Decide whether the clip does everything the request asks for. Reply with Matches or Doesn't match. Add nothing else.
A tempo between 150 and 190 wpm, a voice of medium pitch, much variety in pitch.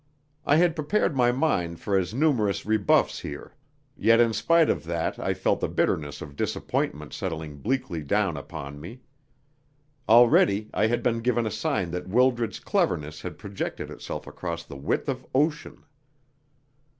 Doesn't match